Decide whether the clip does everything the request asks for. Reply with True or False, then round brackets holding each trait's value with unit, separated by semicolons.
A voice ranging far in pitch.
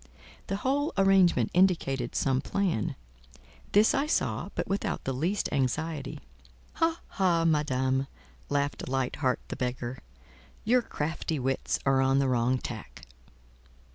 True (6.7 semitones)